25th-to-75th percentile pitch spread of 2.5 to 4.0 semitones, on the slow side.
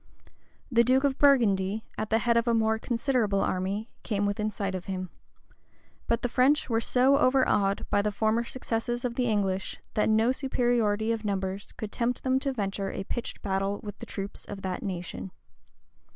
No: average, 3.5 semitones; average, 185 wpm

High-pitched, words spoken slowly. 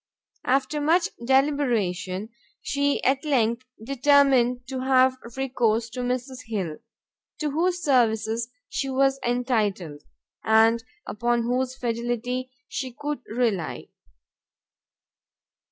Yes: very high, 250 Hz; slow, 100 wpm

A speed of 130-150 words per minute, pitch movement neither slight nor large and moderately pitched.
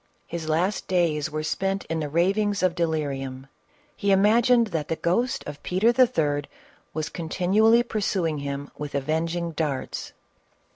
Yes: average, 145 wpm; average, 4.7 semitones; medium, 170 Hz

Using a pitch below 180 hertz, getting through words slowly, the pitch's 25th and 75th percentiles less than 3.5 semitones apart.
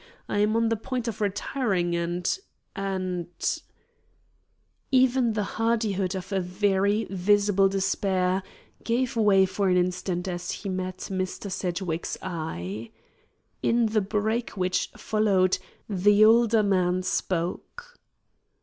No: high, 195 Hz; slow, 120 wpm; average, 2.9 semitones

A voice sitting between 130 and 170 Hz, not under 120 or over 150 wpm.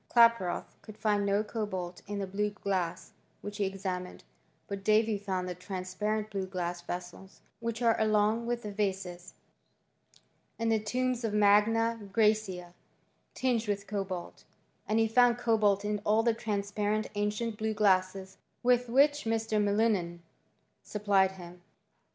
No: high, 210 Hz; average, 140 wpm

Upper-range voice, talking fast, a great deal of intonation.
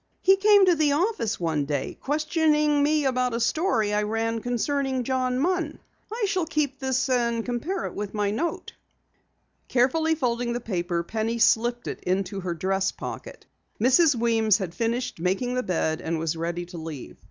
No: high, 240 Hz; average, 175 wpm; wide, 6.8 semitones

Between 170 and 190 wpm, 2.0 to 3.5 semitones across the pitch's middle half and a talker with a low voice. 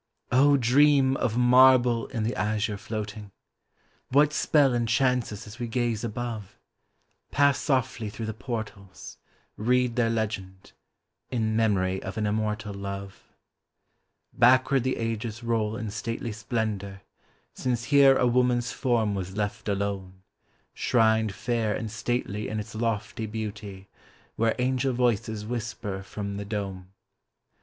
No: slow, 135 wpm; average, 2.9 semitones; low, 110 Hz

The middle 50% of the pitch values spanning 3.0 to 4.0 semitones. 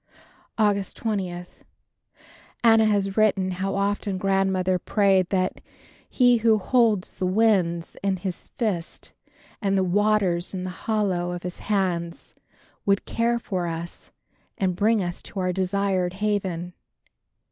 No: narrow, 2.5 semitones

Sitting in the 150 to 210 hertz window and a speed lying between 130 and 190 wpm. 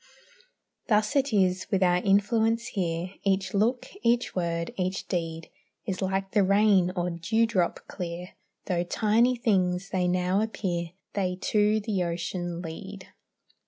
Yes: high, 190 Hz; slow, 135 wpm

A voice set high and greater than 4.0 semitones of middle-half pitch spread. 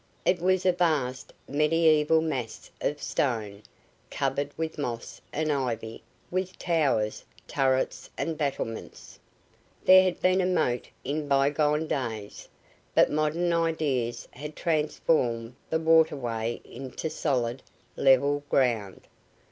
No: medium, 145 Hz; average, 4.5 semitones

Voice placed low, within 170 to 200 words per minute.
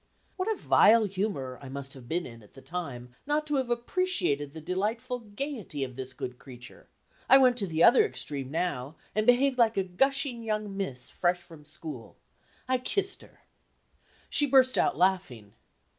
No: medium, 185 Hz; average, 175 wpm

